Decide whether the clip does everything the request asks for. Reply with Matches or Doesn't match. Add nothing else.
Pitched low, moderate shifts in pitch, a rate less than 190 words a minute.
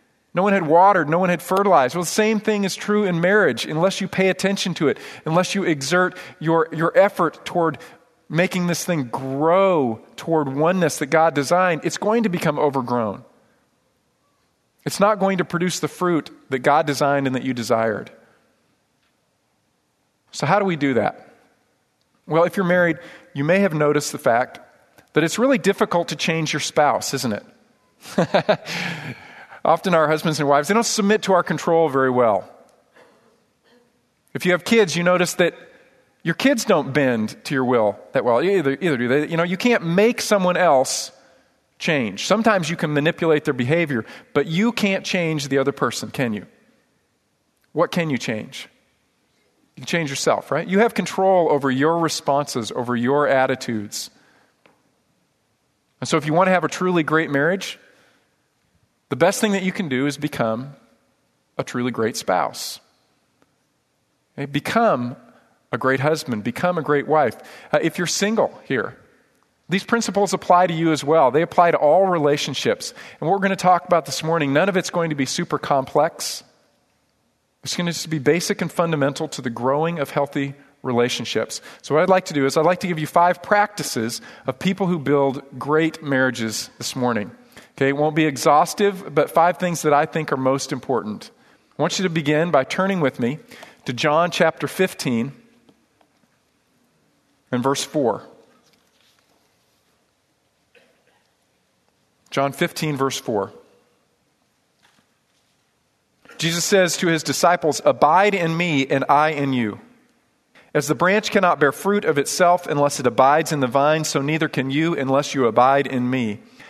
Doesn't match